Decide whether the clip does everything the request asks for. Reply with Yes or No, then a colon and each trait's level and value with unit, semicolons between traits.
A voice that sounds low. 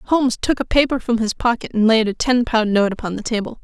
No: high, 230 Hz